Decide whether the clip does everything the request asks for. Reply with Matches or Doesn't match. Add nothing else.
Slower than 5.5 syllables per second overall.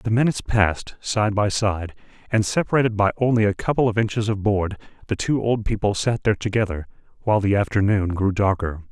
Doesn't match